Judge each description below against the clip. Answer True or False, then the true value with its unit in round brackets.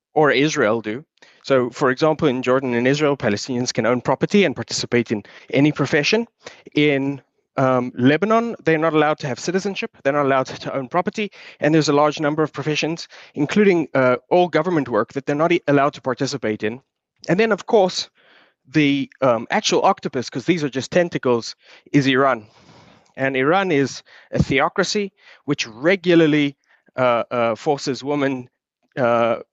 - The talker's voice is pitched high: False (140 Hz)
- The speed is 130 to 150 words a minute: False (165 wpm)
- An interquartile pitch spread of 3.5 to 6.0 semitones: True (4.1 semitones)